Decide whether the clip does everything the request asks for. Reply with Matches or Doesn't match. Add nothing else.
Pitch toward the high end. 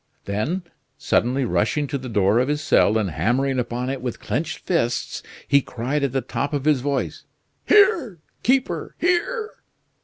Doesn't match